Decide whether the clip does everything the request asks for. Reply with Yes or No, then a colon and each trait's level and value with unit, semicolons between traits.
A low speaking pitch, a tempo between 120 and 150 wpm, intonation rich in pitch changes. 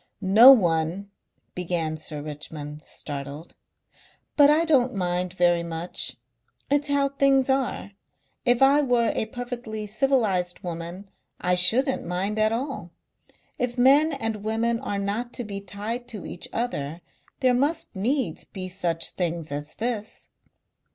No: high, 210 Hz; average, 140 wpm; wide, 6.2 semitones